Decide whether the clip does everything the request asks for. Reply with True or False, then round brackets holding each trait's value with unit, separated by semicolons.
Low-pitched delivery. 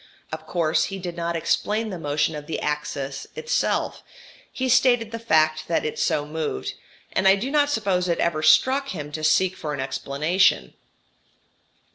False (170 Hz)